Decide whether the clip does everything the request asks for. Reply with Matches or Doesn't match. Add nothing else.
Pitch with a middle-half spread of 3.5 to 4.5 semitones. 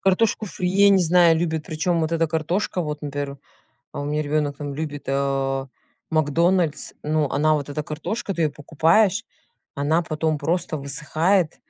Doesn't match